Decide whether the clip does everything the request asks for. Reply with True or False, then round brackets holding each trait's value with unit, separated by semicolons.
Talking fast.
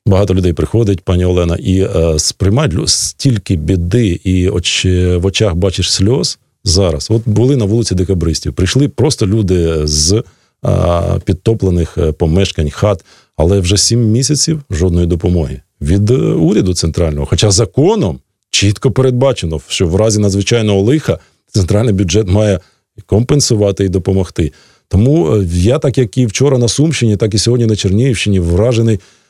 False (140 wpm)